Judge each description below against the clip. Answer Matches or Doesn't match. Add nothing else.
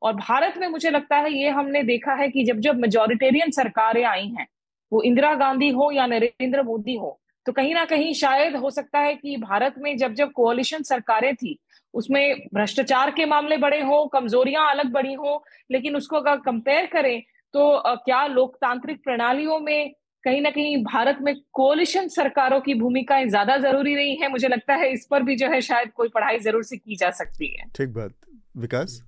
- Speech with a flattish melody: Doesn't match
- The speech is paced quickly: Matches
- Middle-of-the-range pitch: Doesn't match